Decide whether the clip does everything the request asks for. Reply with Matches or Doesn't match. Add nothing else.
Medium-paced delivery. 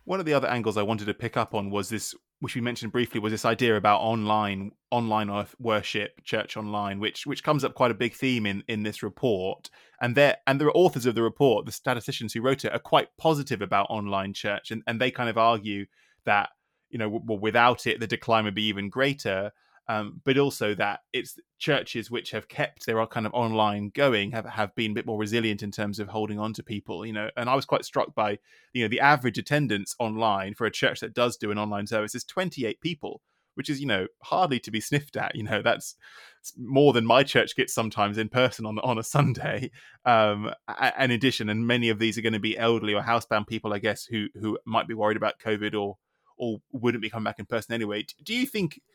Doesn't match